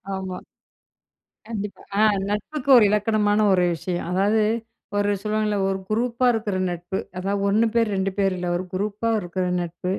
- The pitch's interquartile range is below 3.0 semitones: Yes, narrow, 2.4 semitones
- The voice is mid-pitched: No, high, 205 Hz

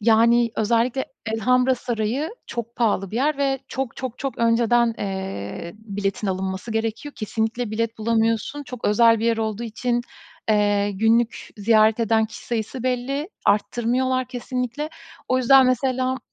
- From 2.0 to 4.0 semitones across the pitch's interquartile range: Yes, narrow, 2.6 semitones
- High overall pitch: Yes, high, 230 Hz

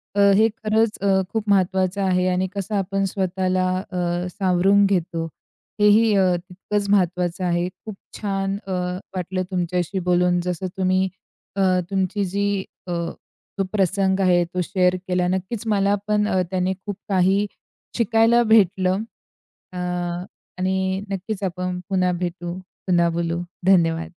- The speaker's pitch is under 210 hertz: Yes, medium, 185 Hz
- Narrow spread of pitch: Yes, narrow, 1.9 semitones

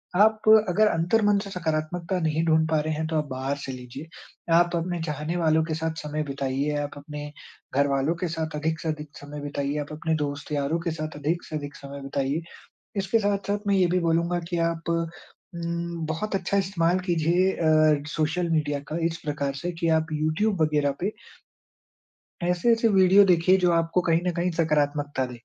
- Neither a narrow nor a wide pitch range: Yes, average, 3.0 semitones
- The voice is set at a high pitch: No, medium, 160 Hz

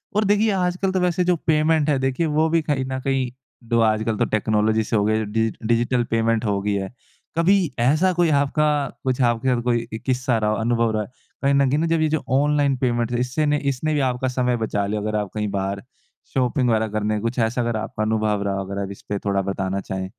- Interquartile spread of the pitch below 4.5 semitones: No, average, 5.2 semitones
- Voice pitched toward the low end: Yes, low, 120 Hz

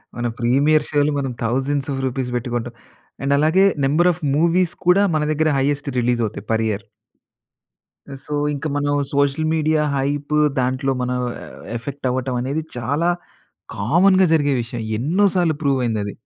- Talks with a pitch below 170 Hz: Yes, medium, 140 Hz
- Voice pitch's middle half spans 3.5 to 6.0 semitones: Yes, average, 3.8 semitones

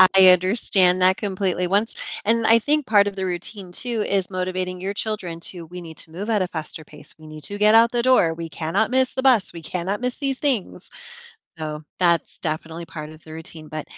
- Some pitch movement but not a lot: Yes, average, 4.5 semitones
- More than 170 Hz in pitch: Yes, medium, 185 Hz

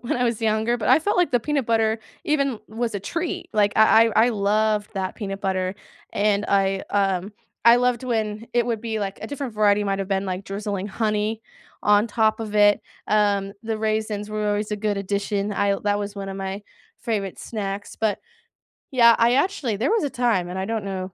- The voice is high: Yes, high, 210 Hz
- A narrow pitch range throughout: Yes, narrow, 2.3 semitones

